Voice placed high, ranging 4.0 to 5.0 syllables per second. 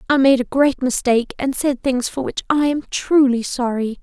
Yes: very high, 260 Hz; 4.9 syllables/s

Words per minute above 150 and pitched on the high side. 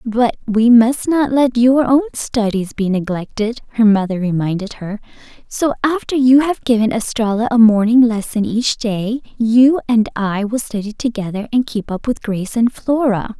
Yes: average, 170 wpm; high, 230 Hz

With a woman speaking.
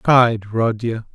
No: male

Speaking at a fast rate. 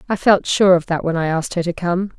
Yes: fast, 300 wpm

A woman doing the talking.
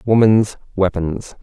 No: male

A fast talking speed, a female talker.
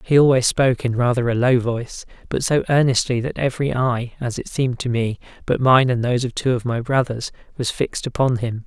No: fast, 220 wpm; male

